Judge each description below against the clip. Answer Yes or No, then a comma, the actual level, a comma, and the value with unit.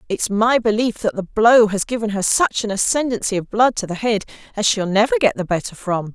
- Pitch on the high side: Yes, high, 215 Hz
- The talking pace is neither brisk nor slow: No, fast, 235 wpm